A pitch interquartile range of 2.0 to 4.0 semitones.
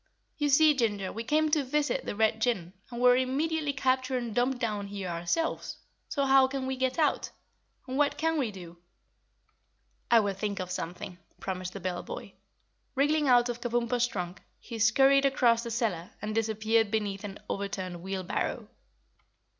No: average, 5.1 semitones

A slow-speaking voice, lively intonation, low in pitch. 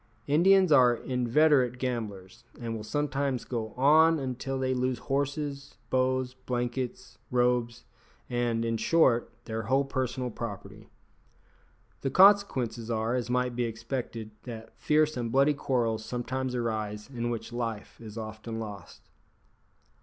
No: slow, 130 wpm; narrow, 2.6 semitones; low, 125 Hz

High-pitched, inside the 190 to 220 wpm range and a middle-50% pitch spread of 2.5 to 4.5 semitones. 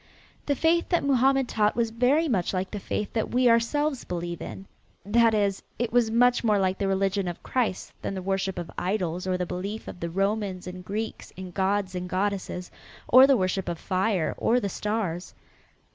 Yes: high, 200 Hz; average, 195 wpm; average, 4.0 semitones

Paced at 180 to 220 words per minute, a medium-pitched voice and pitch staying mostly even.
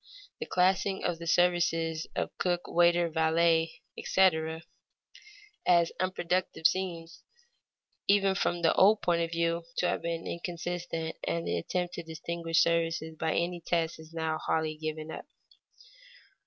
No: average, 140 wpm; medium, 170 Hz; narrow, 1.5 semitones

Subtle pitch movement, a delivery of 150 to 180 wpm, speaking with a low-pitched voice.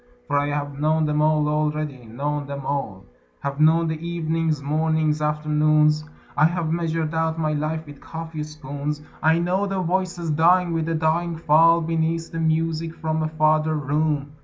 No: narrow, 1.5 semitones; average, 170 wpm; medium, 155 Hz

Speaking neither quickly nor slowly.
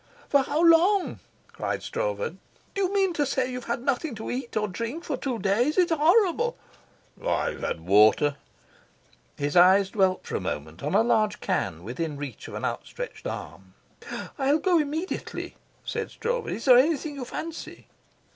Yes: average, 165 wpm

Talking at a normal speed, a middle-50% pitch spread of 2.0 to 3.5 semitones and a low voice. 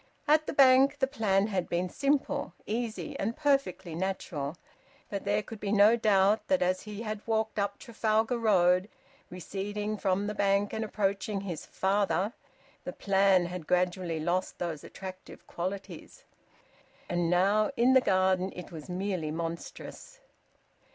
No: average, 145 wpm; average, 3.1 semitones; high, 200 Hz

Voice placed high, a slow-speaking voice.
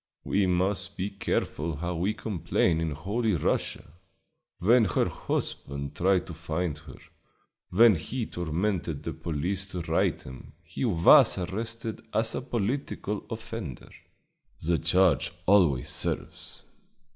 No: very low, 90 Hz; slow, 125 wpm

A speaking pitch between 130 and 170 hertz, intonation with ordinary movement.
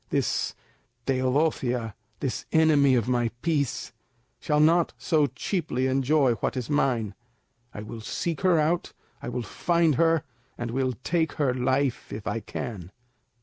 Yes: low, 135 Hz; average, 4.5 semitones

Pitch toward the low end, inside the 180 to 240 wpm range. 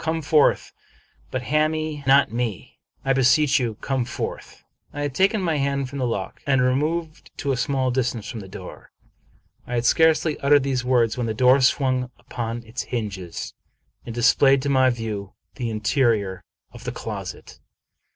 No: low, 130 Hz; average, 170 wpm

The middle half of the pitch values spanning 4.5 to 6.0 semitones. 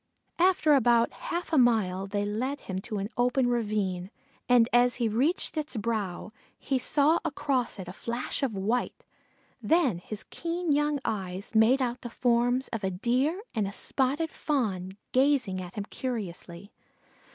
Yes: average, 5.2 semitones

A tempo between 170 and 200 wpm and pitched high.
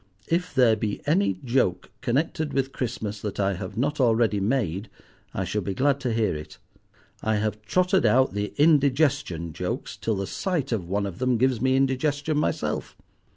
No: average, 175 wpm; low, 120 Hz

